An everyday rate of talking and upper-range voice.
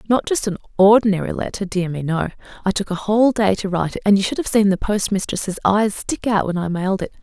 No: fast, 250 wpm; high, 200 Hz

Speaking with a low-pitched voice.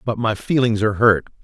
Yes: low, 110 Hz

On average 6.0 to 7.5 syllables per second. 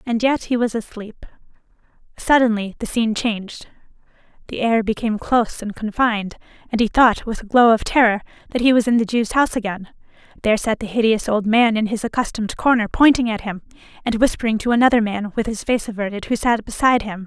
Yes: 6.2 syllables/s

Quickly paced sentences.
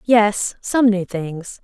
No: average, 145 wpm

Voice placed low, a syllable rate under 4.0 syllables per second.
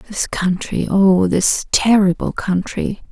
No: high, 190 Hz; 3.6 syllables/s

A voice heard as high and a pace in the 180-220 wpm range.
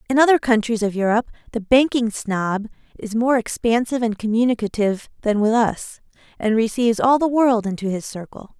No: high, 230 Hz; average, 170 wpm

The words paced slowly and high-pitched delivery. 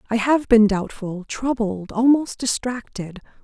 Yes: slow, 120 wpm; high, 225 Hz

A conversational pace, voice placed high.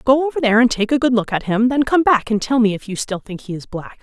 No: fast, 345 wpm; high, 235 Hz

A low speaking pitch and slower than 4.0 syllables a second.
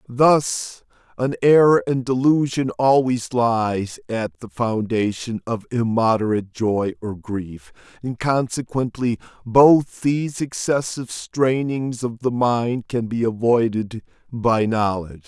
Yes: low, 120 Hz; 3.8 syllables/s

